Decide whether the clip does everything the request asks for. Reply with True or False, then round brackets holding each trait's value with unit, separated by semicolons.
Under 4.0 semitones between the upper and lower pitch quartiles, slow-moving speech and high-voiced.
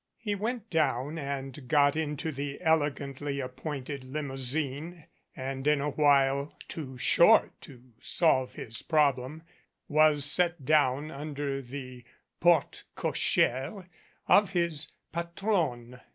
False (3.0 semitones; 110 wpm; 145 Hz)